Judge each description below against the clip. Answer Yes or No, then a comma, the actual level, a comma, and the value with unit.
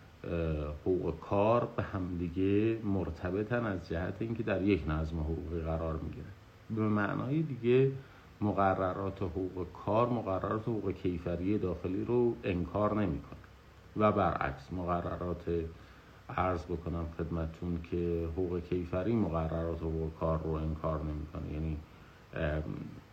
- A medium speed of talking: Yes, average, 115 wpm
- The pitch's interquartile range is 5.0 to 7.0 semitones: No, average, 3.6 semitones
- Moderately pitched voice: No, very low, 90 Hz